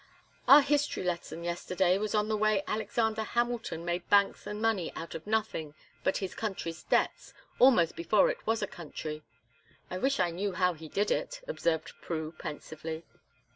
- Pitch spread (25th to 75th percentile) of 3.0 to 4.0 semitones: No, average, 4.6 semitones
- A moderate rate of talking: Yes, average, 170 wpm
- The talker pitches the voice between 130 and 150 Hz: No, high, 190 Hz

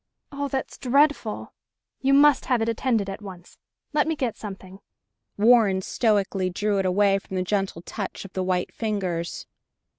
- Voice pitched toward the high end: Yes, high, 205 Hz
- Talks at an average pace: Yes, average, 160 wpm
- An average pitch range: Yes, average, 4.6 semitones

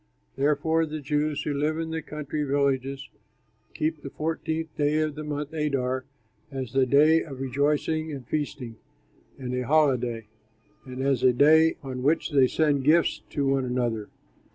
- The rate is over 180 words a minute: No, average, 160 wpm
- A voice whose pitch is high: No, medium, 145 Hz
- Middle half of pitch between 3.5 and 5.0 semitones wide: No, average, 2.7 semitones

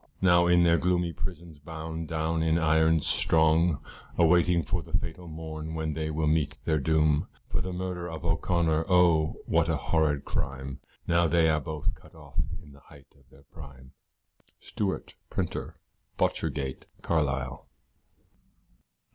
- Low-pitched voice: Yes, very low, 80 Hz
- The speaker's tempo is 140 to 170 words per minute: Yes, average, 145 wpm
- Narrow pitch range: Yes, narrow, 2.1 semitones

